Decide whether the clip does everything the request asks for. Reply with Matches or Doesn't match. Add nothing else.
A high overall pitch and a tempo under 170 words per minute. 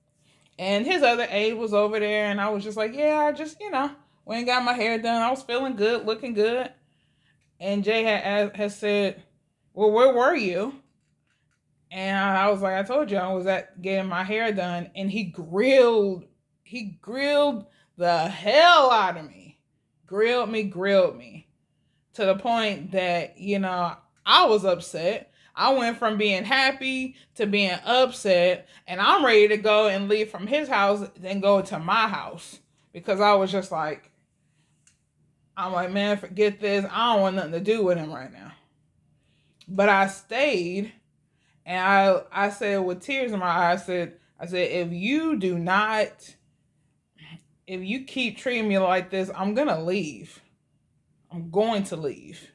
Doesn't match